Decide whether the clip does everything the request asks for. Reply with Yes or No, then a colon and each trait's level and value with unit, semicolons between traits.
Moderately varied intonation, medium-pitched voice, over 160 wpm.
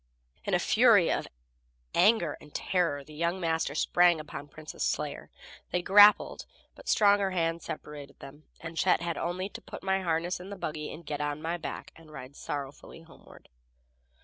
Yes: average, 3.1 semitones; medium, 165 Hz; average, 170 wpm